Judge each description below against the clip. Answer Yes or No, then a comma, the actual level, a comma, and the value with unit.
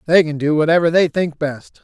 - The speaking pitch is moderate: Yes, medium, 160 Hz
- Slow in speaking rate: No, fast, 230 wpm